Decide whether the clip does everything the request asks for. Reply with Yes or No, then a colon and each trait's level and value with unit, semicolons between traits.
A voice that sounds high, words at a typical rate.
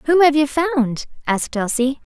Yes: very high, 280 Hz; average, 165 wpm